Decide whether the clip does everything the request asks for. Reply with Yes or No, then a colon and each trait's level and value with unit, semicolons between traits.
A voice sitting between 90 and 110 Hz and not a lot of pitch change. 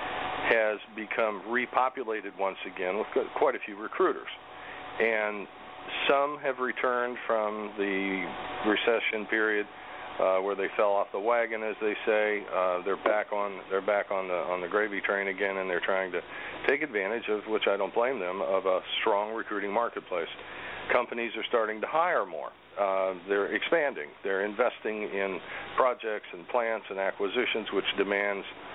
Yes: low, 105 Hz; narrow, 2.2 semitones